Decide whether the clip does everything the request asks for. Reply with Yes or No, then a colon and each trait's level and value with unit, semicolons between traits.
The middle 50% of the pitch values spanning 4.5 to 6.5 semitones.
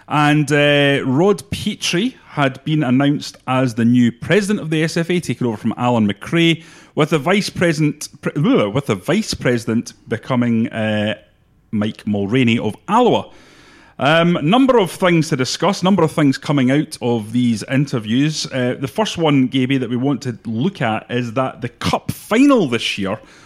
Yes: average, 5.2 semitones